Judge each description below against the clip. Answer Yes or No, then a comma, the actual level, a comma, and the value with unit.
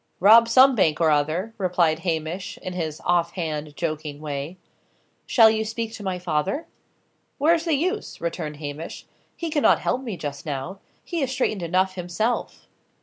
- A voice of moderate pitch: Yes, medium, 180 Hz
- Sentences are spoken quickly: No, average, 160 wpm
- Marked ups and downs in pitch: Yes, wide, 6.3 semitones